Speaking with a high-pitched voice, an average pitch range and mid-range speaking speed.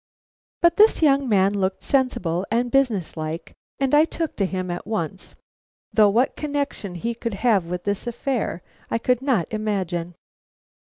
No: high, 215 Hz; wide, 6.2 semitones; average, 160 wpm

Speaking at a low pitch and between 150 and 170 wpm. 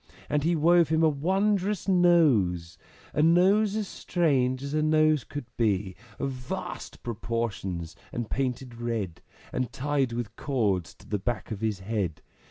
Yes: low, 130 Hz; average, 155 wpm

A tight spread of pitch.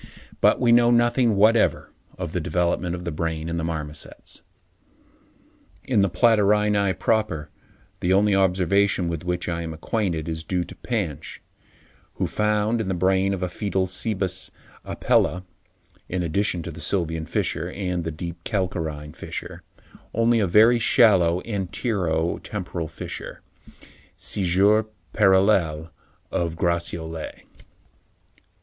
No: average, 3.8 semitones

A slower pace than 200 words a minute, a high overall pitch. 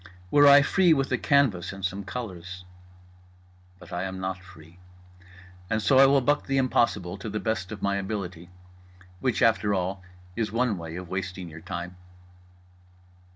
No: average, 165 wpm; low, 100 Hz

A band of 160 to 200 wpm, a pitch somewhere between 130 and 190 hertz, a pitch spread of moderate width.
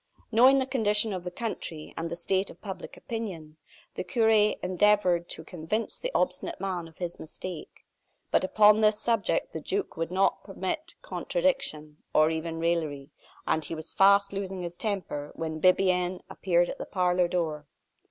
Yes: average, 165 wpm; medium, 185 Hz; average, 4.1 semitones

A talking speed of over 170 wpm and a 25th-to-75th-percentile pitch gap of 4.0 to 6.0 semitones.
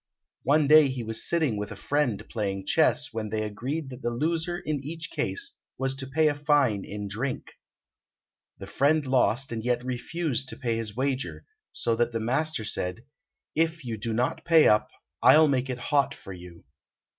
Yes: average, 185 wpm; average, 4.9 semitones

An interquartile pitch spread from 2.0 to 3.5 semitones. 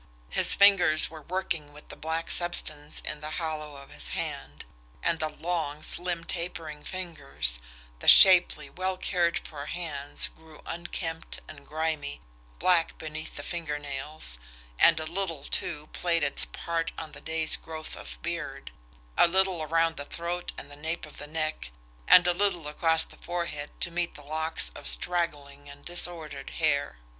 Yes: average, 2.7 semitones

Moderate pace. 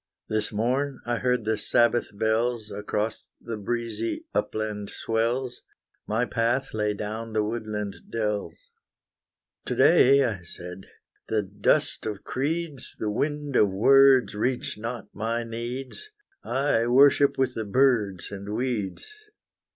No: slow, 130 wpm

